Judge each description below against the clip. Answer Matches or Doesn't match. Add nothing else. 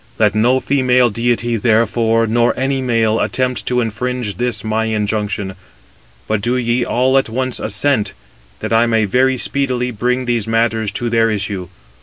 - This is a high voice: Doesn't match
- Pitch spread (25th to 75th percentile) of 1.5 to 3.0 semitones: Matches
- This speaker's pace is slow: Doesn't match